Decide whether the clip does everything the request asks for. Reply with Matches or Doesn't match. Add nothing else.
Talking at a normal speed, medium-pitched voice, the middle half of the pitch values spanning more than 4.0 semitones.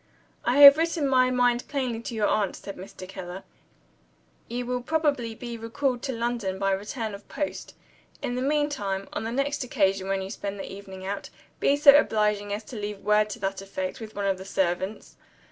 Doesn't match